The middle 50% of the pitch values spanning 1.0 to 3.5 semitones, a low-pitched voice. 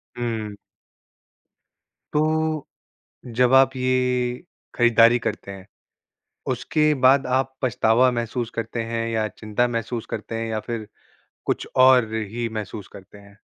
Yes: narrow, 2.5 semitones; low, 120 Hz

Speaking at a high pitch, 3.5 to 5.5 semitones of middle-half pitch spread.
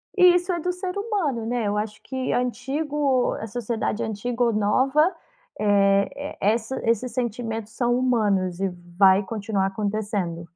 Yes: high, 230 Hz; average, 4.4 semitones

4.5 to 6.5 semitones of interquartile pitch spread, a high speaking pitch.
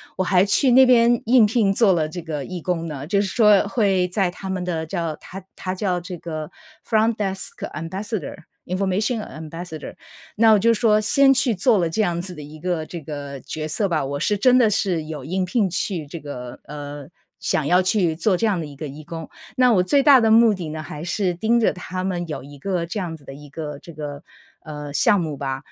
No: average, 5.1 semitones; medium, 180 Hz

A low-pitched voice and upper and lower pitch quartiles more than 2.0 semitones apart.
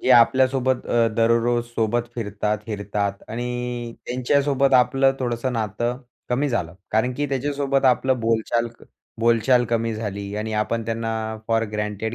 Yes: low, 115 Hz; narrow, 2.5 semitones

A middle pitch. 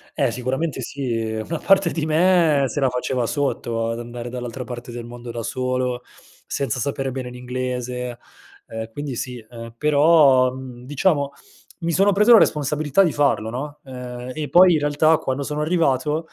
No: low, 130 Hz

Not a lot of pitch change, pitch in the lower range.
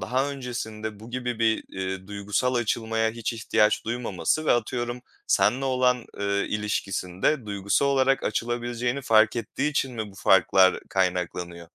No: average, 3.6 semitones; low, 115 Hz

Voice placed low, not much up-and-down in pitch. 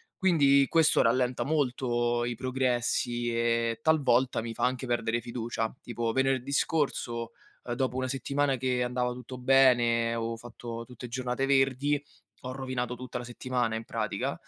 Yes: low, 125 Hz; narrow, 1.9 semitones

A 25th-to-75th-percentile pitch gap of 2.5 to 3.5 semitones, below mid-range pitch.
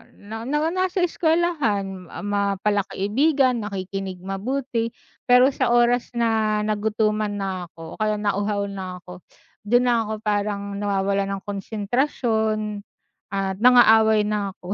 No: average, 3.2 semitones; high, 210 Hz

